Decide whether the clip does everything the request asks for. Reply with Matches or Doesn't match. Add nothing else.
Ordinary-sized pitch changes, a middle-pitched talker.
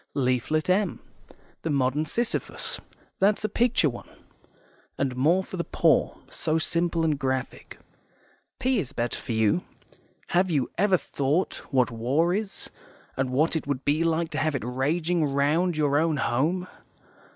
Matches